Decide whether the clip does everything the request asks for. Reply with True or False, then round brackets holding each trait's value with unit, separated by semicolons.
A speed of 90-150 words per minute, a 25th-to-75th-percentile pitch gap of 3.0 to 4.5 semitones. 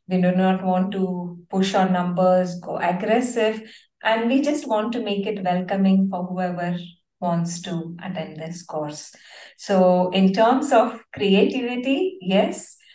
True (145 wpm; 3.6 semitones)